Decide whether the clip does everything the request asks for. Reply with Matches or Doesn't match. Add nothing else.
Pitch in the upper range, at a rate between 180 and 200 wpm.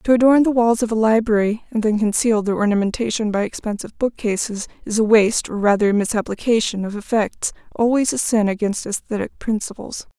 Doesn't match